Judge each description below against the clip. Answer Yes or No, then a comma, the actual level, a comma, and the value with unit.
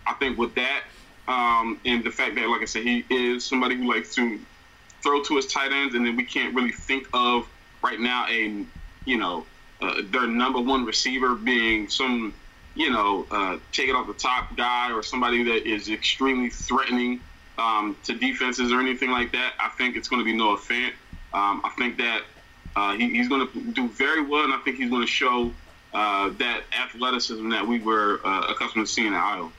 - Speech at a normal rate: No, fast, 210 wpm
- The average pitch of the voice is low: Yes, low, 125 Hz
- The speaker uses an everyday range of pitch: No, narrow, 2.1 semitones